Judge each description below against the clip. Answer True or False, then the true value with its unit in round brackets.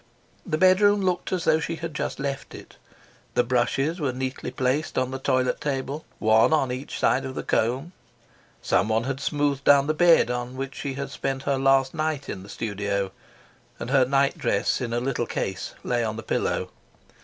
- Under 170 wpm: False (190 wpm)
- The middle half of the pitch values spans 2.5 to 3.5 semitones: True (3.0 semitones)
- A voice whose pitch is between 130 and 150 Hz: True (135 Hz)